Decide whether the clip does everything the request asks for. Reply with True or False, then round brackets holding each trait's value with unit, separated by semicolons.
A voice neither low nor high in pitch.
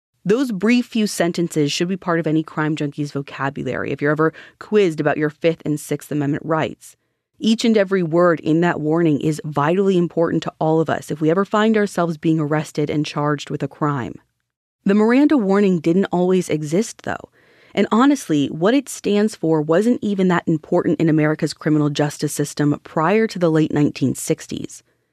True (160 Hz)